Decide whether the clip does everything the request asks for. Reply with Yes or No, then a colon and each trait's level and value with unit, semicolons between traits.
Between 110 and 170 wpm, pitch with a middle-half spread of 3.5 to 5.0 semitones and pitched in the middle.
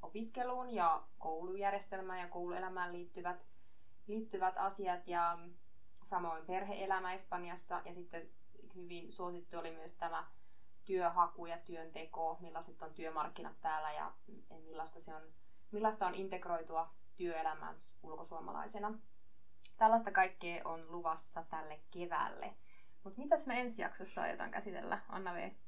No: average, 115 wpm; narrow, 2.6 semitones; medium, 175 Hz